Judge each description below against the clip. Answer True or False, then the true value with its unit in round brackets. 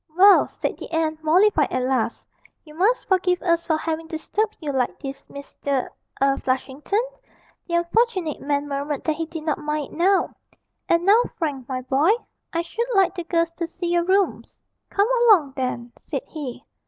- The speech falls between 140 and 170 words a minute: False (180 wpm)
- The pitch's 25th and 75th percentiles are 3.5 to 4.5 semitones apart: True (4.2 semitones)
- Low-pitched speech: False (320 Hz)